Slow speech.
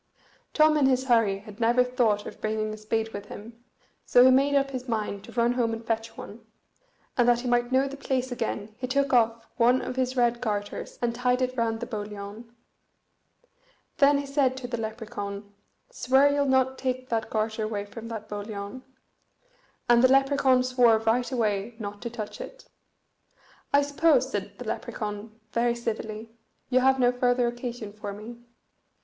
No: average, 180 wpm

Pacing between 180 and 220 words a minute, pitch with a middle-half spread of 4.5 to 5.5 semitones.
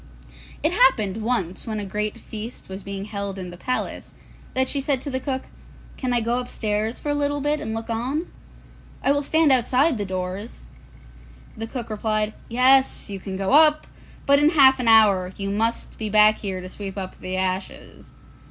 Yes: average, 190 wpm; average, 5.0 semitones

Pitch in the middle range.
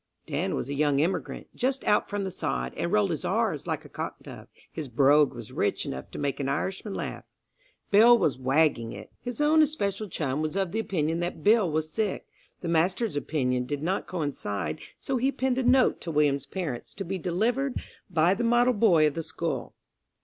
Yes: medium, 170 Hz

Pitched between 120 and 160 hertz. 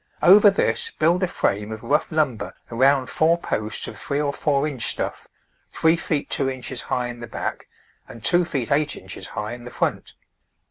Yes: medium, 140 Hz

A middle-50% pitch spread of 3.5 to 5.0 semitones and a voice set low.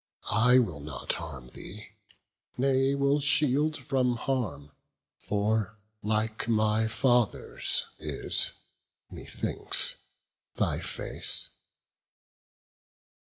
Yes: average, 4.0 semitones; low, 115 Hz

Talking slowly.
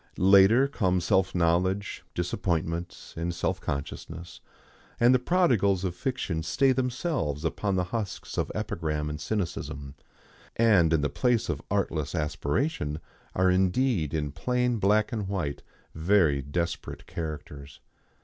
Yes: slow, 130 wpm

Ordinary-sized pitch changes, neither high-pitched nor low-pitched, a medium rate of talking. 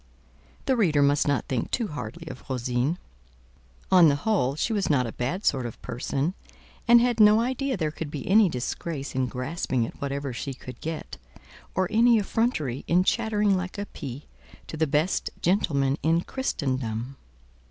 No: wide, 7.3 semitones; medium, 155 Hz; average, 170 wpm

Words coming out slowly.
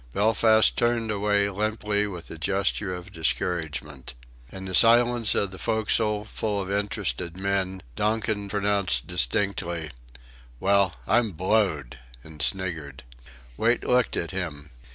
Yes: slow, 125 wpm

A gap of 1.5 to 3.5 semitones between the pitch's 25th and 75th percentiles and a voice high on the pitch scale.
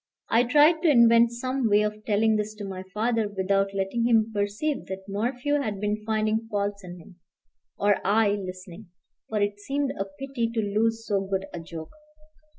Yes: average, 2.8 semitones; high, 210 Hz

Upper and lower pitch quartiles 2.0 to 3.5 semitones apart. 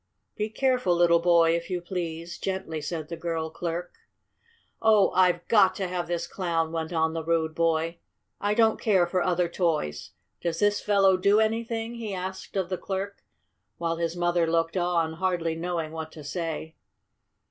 Yes: narrow, 2.5 semitones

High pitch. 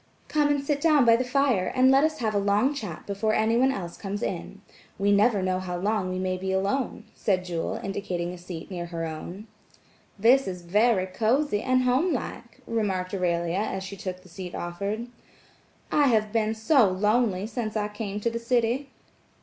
Yes: high, 210 Hz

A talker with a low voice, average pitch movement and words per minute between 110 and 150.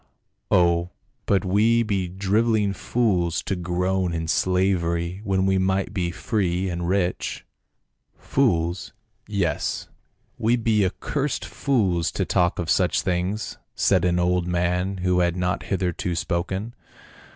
No: very low, 95 Hz; narrow, 2.3 semitones; average, 140 wpm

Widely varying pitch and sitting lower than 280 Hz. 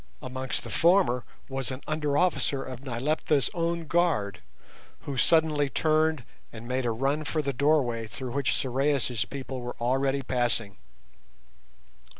No: average, 3.7 semitones; low, 135 Hz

